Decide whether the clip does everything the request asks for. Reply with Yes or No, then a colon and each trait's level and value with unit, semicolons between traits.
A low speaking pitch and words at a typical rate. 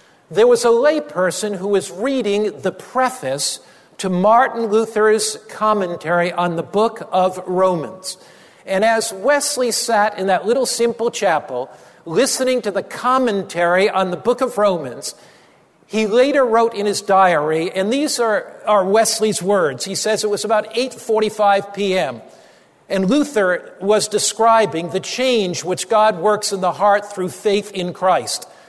No: high, 205 Hz; average, 150 wpm